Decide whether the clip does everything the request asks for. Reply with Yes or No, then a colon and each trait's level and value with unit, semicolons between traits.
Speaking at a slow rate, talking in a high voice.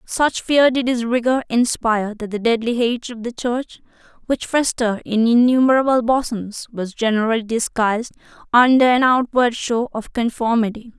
No: average, 150 wpm; high, 235 Hz